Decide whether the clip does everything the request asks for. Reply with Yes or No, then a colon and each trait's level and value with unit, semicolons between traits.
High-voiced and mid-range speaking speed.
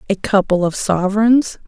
Yes: high, 200 Hz; average, 145 wpm